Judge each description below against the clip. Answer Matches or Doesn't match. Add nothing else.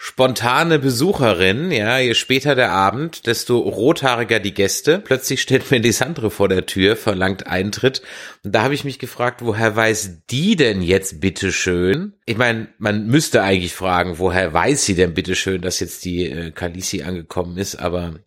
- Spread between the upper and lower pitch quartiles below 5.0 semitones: Doesn't match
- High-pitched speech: Doesn't match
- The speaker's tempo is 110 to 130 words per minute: Doesn't match